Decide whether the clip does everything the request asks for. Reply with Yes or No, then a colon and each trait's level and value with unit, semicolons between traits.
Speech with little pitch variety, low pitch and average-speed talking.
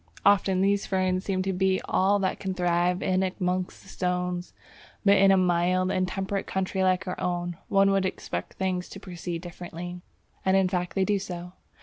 No: narrow, 1.3 semitones; medium, 185 Hz; average, 190 wpm